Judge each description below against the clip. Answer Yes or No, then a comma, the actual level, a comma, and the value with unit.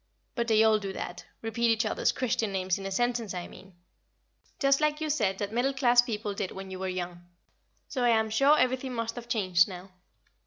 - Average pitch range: Yes, average, 4.2 semitones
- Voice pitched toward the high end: Yes, high, 220 Hz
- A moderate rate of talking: No, fast, 210 wpm